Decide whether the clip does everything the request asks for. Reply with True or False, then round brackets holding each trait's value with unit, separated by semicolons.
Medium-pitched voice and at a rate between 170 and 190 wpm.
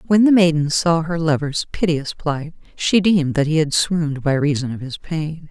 False (160 Hz; 205 wpm)